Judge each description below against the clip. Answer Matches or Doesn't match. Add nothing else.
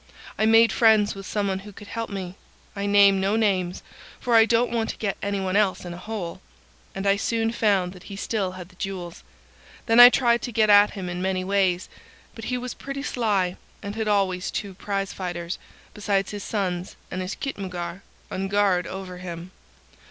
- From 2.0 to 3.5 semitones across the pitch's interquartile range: Matches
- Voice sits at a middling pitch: Doesn't match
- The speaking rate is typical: Matches